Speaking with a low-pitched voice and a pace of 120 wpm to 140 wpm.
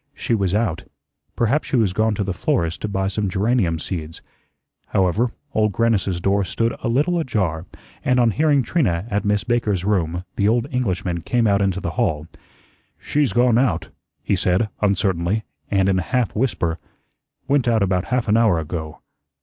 No: low, 100 Hz; average, 175 wpm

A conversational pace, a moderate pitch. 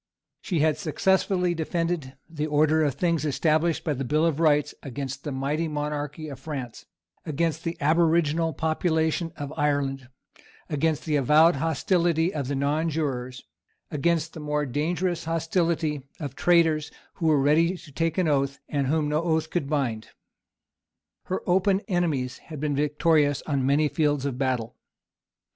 Yes: average, 150 wpm; medium, 155 Hz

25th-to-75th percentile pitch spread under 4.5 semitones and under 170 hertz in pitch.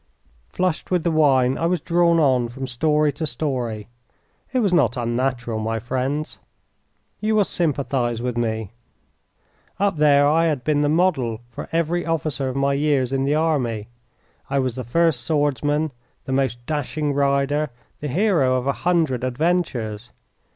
Yes: average, 4.0 semitones; medium, 140 Hz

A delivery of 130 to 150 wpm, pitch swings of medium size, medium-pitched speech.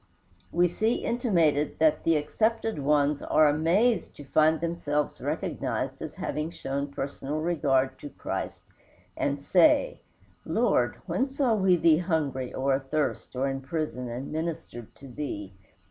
Yes: average, 140 wpm; average, 3.8 semitones; medium, 150 Hz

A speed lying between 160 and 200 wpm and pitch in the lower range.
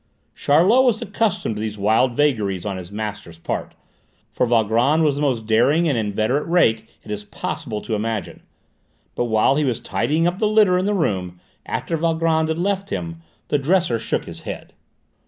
Yes: average, 180 wpm; low, 125 Hz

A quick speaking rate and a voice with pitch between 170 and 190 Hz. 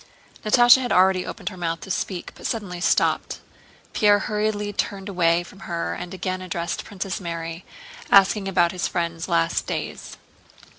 No: average, 155 wpm; medium, 185 Hz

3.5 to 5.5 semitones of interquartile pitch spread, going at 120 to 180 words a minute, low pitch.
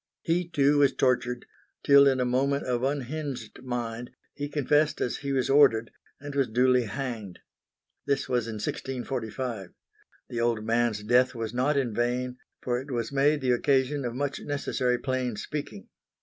No: average, 2.8 semitones; average, 165 wpm; low, 125 Hz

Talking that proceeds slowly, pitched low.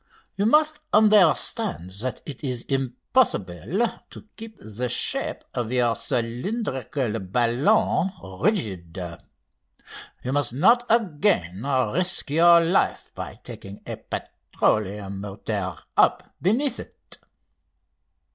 Yes: slow, 100 wpm; low, 130 Hz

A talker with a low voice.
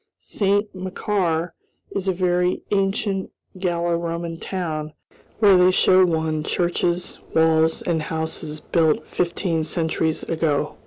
No: medium, 170 Hz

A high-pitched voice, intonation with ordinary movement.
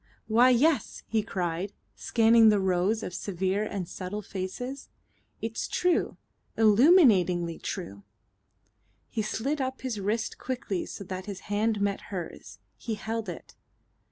Yes: high, 210 Hz; average, 3.6 semitones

